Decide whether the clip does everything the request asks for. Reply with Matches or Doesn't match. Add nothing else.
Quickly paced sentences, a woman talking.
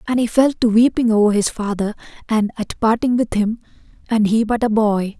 Matches